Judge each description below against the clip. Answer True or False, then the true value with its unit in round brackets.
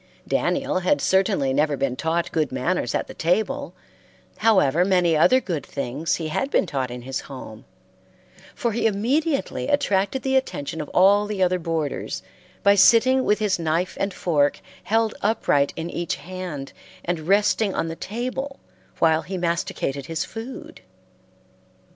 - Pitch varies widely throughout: True (5.8 semitones)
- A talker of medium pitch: True (180 Hz)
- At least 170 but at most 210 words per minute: False (155 wpm)